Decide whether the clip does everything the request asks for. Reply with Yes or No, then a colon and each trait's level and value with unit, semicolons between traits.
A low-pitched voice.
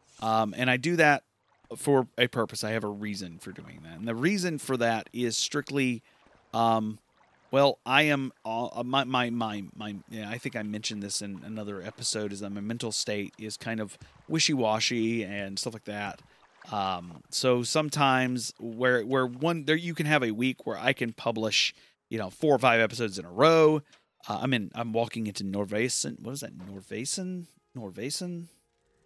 Yes: low, 115 Hz